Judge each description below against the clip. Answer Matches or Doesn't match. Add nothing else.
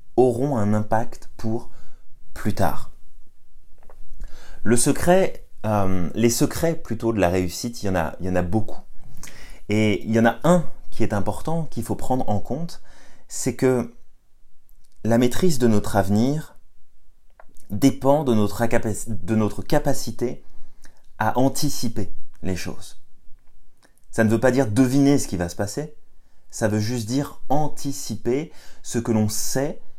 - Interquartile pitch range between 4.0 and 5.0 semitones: Matches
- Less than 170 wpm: Matches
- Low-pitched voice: Matches